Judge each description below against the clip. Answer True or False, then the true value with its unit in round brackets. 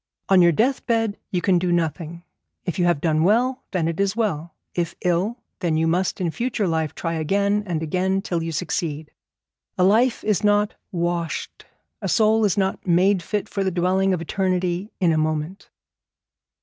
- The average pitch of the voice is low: False (180 Hz)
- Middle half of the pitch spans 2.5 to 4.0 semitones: True (3.3 semitones)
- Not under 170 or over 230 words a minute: True (185 wpm)